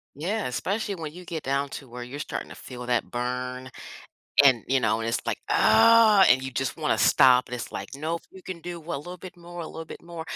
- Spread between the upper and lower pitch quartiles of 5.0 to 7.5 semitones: Yes, wide, 5.6 semitones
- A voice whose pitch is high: No, medium, 145 Hz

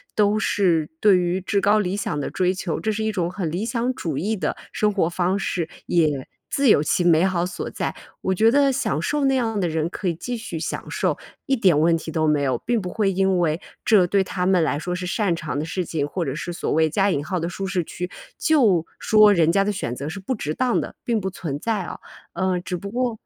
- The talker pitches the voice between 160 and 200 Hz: Yes, medium, 185 Hz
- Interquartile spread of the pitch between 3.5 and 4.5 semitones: Yes, average, 4.1 semitones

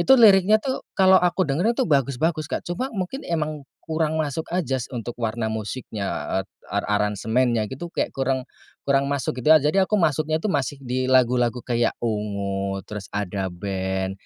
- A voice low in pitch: Yes, low, 130 Hz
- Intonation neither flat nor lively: No, wide, 6.9 semitones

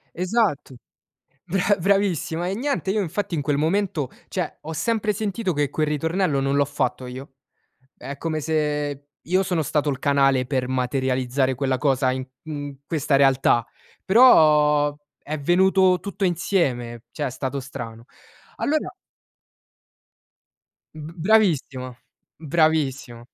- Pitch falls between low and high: Yes, medium, 150 Hz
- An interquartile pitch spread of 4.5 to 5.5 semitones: Yes, average, 5.1 semitones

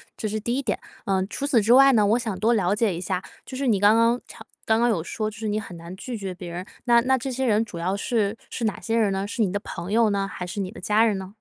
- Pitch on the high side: Yes, high, 215 Hz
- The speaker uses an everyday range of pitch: Yes, average, 3.3 semitones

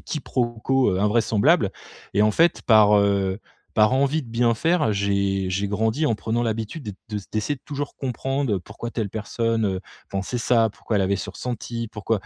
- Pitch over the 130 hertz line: No, low, 110 Hz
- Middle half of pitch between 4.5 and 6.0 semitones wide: No, average, 3.4 semitones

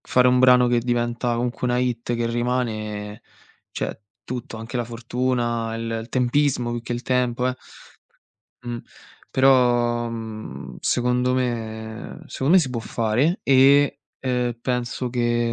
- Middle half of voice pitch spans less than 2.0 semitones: Yes, narrow, 1.4 semitones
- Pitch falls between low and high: No, low, 120 Hz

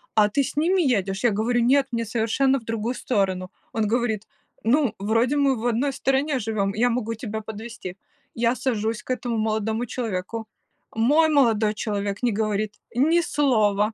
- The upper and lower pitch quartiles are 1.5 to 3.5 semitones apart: Yes, average, 3.1 semitones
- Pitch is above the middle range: Yes, high, 230 Hz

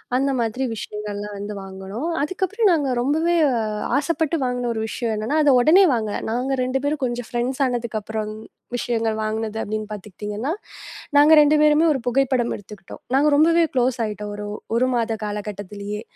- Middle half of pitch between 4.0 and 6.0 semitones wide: Yes, average, 4.9 semitones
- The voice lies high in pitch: Yes, high, 240 Hz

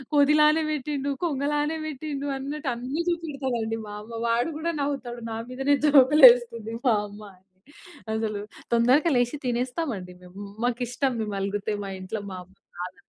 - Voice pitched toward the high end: Yes, very high, 250 Hz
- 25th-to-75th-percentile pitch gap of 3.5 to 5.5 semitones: Yes, average, 4.7 semitones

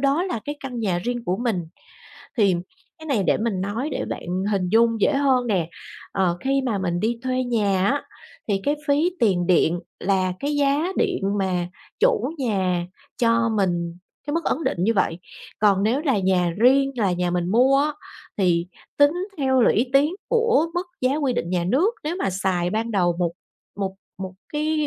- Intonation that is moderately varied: No, wide, 6.9 semitones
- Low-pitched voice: No, high, 230 Hz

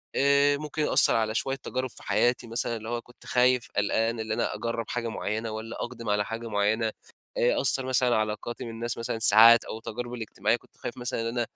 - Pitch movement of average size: No, narrow, 1.9 semitones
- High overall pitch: No, low, 115 Hz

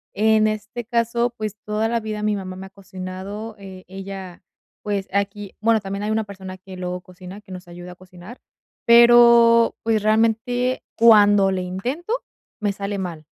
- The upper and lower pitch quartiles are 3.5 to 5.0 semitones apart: No, average, 3.0 semitones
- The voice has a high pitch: Yes, high, 205 Hz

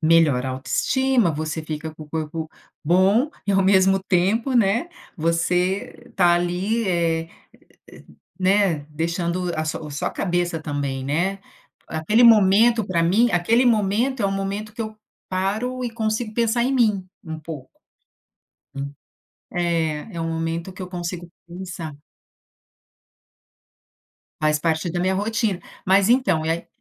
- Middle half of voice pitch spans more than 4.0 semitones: Yes, average, 4.5 semitones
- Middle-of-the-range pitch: Yes, medium, 180 Hz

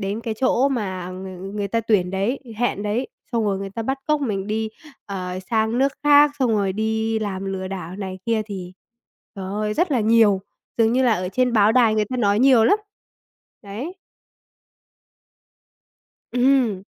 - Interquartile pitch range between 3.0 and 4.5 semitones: Yes, average, 3.8 semitones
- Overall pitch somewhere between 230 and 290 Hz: No, high, 215 Hz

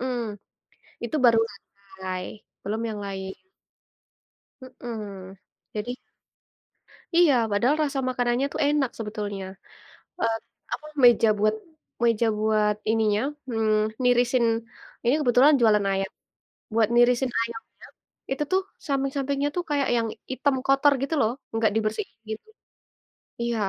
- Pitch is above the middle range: Yes, high, 230 Hz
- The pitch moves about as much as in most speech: Yes, average, 3.6 semitones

